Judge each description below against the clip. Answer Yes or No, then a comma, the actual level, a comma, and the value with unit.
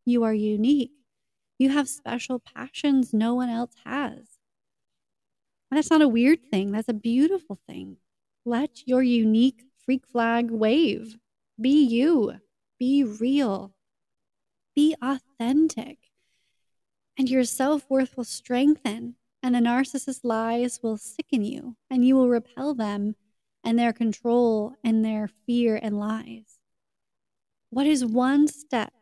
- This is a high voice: Yes, high, 245 Hz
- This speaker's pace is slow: Yes, slow, 125 wpm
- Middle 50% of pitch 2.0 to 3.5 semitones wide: Yes, average, 3.2 semitones